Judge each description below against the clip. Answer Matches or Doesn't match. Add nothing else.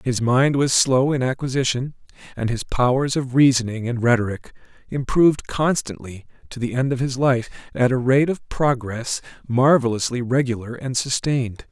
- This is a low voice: Matches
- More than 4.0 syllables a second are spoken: Matches